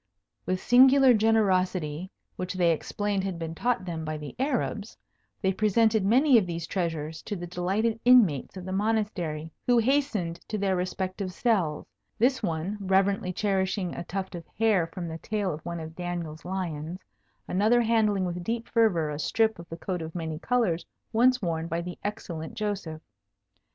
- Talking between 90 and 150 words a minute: No, average, 170 wpm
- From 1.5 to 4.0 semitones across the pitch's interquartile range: No, average, 4.6 semitones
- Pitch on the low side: No, medium, 185 Hz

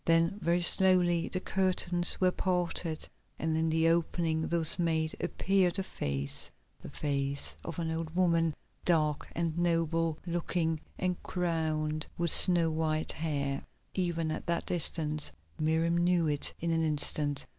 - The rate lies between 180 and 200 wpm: No, average, 145 wpm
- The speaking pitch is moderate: Yes, medium, 165 Hz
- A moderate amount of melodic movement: No, narrow, 1.8 semitones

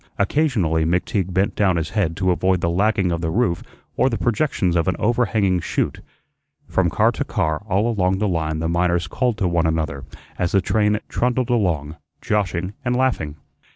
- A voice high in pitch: No, very low, 95 Hz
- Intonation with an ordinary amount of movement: Yes, average, 4.4 semitones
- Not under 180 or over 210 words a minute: Yes, average, 185 wpm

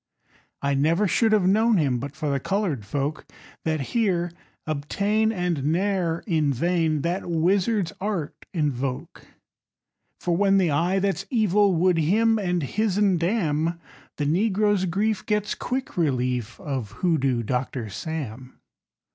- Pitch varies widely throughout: Yes, wide, 5.7 semitones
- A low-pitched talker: No, medium, 170 Hz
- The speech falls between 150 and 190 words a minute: No, average, 140 wpm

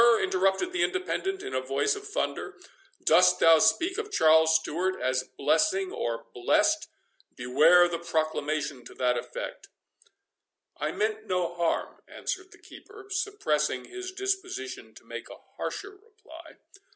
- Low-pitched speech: No, medium, 185 Hz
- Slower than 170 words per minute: Yes, slow, 135 wpm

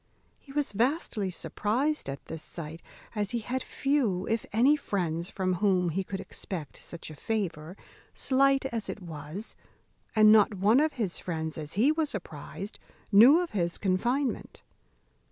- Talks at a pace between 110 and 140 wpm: No, average, 155 wpm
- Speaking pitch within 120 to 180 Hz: No, high, 205 Hz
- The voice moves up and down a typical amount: No, wide, 6.4 semitones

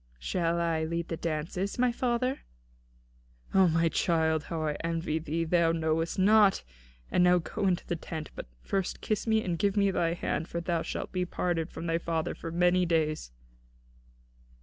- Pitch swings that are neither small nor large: No, narrow, 2.2 semitones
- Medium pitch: Yes, medium, 170 Hz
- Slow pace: No, average, 180 wpm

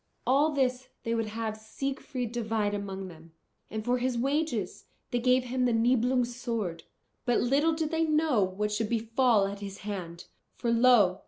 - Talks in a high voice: Yes, high, 235 Hz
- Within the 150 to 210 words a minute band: Yes, average, 170 wpm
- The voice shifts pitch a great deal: No, average, 3.5 semitones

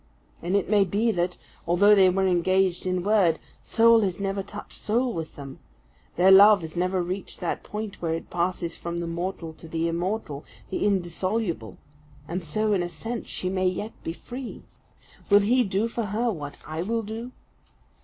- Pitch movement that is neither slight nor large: Yes, average, 3.5 semitones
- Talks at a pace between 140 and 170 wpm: No, average, 185 wpm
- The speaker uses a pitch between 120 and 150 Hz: No, medium, 185 Hz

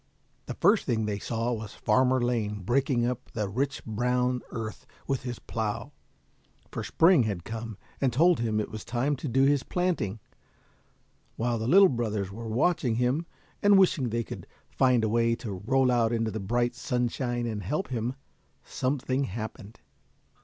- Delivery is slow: No, average, 165 wpm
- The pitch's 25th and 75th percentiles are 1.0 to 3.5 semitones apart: Yes, average, 3.0 semitones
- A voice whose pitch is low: Yes, low, 120 Hz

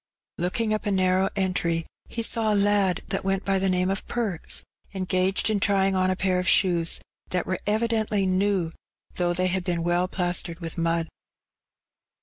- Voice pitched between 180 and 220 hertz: Yes, medium, 185 Hz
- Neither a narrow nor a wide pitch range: No, narrow, 2.0 semitones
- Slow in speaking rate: No, average, 180 wpm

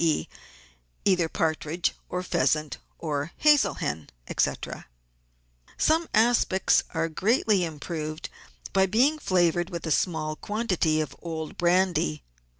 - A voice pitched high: No, medium, 170 Hz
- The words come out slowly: Yes, slow, 115 wpm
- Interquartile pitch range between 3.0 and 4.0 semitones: Yes, average, 3.7 semitones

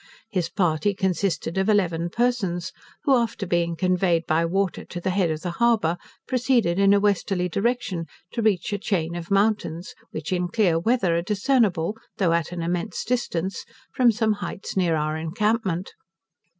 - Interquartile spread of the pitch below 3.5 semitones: No, average, 3.8 semitones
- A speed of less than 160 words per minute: No, average, 165 wpm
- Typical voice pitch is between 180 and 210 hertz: Yes, medium, 185 Hz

